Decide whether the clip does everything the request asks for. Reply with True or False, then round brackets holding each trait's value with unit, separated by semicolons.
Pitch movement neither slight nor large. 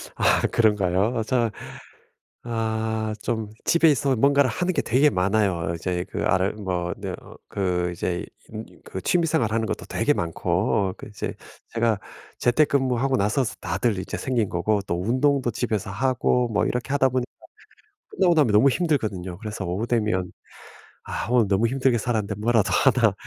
True (4.6 semitones)